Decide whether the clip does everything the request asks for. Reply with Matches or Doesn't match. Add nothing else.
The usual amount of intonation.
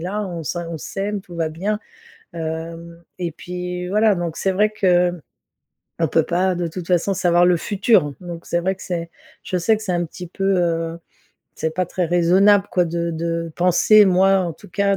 Doesn't match